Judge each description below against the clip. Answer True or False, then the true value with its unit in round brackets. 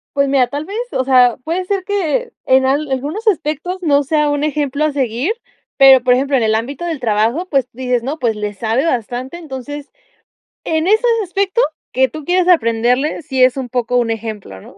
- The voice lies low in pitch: False (275 Hz)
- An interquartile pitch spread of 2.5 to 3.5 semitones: False (4.4 semitones)